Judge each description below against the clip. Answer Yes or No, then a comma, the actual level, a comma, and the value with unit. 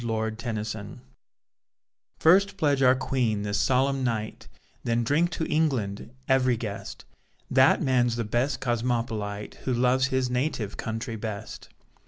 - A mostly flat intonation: No, average, 3.2 semitones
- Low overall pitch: Yes, low, 120 Hz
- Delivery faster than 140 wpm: No, slow, 135 wpm